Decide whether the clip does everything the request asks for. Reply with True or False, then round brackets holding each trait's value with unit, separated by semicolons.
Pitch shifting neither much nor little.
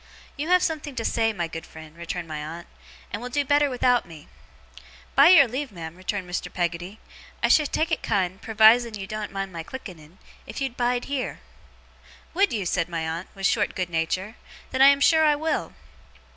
False (7.9 semitones)